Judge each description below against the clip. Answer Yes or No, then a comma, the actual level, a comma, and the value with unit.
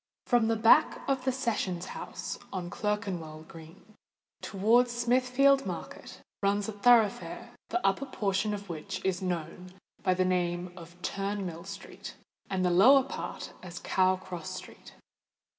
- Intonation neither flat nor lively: Yes, average, 4.1 semitones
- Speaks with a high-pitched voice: Yes, high, 195 Hz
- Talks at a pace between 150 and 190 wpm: No, average, 140 wpm